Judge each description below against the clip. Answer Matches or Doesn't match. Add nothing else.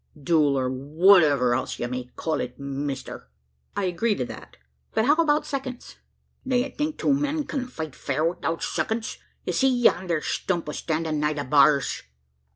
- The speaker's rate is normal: Matches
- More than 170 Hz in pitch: Doesn't match